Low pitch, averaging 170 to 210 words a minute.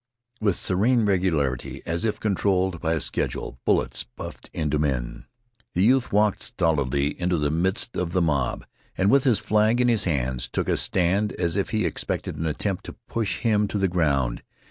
Yes: very low, 90 Hz; average, 185 wpm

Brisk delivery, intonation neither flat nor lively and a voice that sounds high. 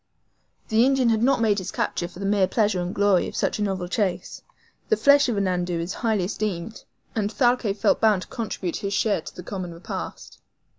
Yes: fast, 210 wpm; average, 3.4 semitones; high, 200 Hz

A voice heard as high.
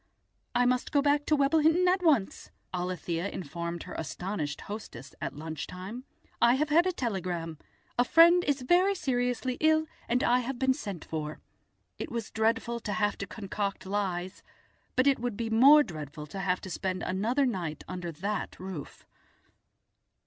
Yes: high, 220 Hz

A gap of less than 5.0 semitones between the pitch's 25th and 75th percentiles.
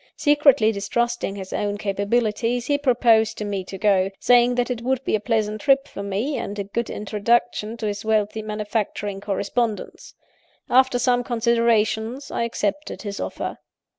Yes: average, 2.9 semitones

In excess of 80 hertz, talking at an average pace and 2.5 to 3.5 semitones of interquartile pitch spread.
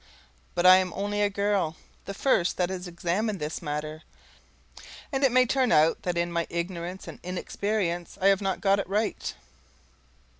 Yes: medium, 185 Hz; average, 175 wpm; average, 3.0 semitones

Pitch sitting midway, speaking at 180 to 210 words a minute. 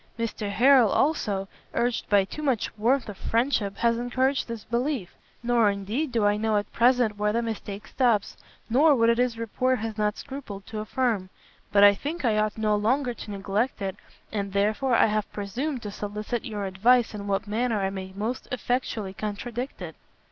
No: high, 220 Hz; average, 185 wpm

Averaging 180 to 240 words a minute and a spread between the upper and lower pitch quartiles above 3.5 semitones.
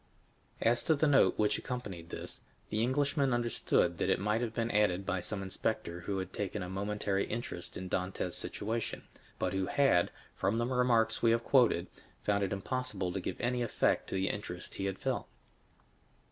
Yes: average, 190 wpm; average, 4.1 semitones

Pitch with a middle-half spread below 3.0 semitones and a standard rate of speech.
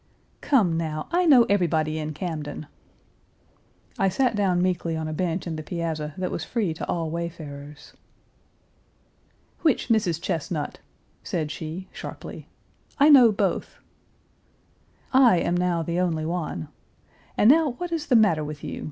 No: average, 5.0 semitones; average, 145 wpm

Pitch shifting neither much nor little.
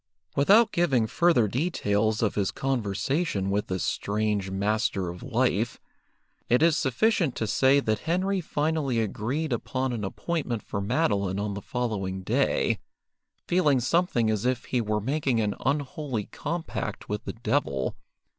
No: wide, 6.0 semitones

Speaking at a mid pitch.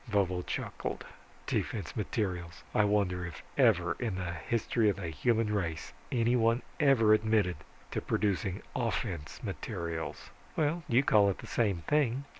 No: low, 105 Hz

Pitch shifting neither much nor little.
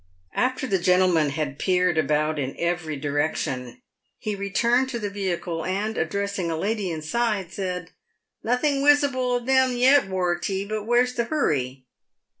No: wide, 6.7 semitones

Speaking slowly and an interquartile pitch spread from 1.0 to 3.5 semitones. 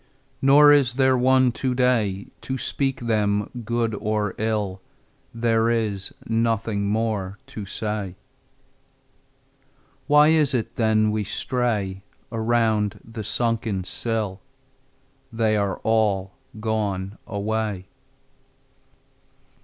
Yes: slow, 100 wpm; narrow, 2.5 semitones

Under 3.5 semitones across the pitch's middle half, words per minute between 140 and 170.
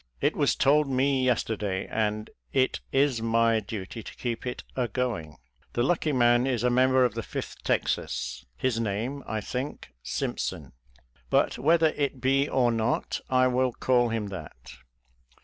Yes: average, 2.9 semitones; average, 160 wpm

